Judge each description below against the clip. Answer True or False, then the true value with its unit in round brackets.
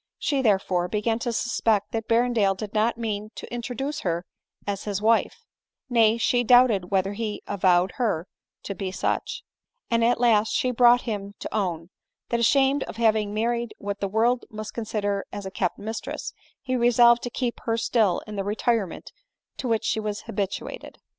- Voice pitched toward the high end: True (220 Hz)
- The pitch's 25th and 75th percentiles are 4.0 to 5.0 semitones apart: False (2.9 semitones)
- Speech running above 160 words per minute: True (180 wpm)